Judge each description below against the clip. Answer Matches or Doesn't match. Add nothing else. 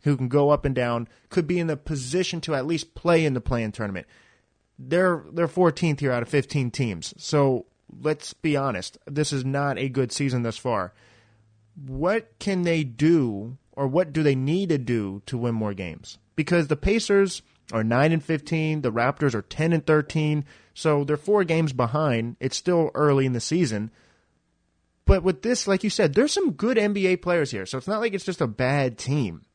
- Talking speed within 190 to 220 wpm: Matches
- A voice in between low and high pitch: Matches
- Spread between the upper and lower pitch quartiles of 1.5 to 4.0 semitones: Doesn't match